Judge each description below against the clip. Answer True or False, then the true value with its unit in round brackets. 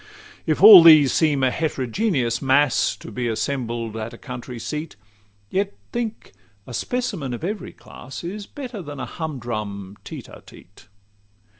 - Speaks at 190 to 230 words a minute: False (155 wpm)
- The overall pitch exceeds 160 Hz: False (140 Hz)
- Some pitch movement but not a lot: False (6.7 semitones)